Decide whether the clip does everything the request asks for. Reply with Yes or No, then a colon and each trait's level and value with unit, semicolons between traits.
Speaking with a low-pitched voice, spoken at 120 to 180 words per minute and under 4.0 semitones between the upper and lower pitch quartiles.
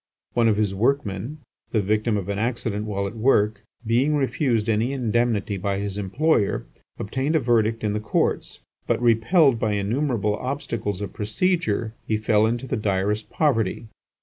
Yes: low, 110 Hz; average, 160 wpm; average, 3.3 semitones